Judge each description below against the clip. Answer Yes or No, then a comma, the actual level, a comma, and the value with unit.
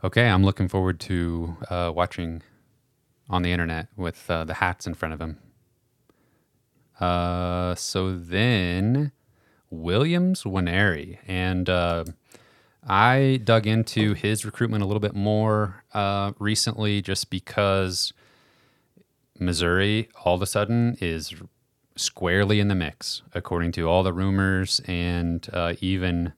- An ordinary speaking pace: No, slow, 125 wpm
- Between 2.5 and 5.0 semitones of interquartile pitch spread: Yes, average, 3.6 semitones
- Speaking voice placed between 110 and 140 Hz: No, very low, 95 Hz